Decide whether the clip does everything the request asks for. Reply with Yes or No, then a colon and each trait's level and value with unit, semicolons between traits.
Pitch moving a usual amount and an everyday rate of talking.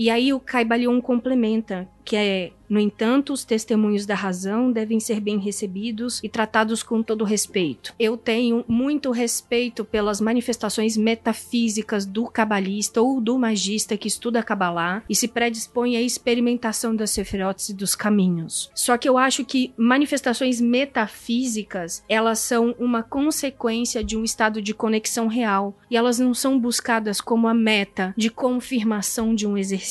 No: narrow, 2.2 semitones; average, 155 wpm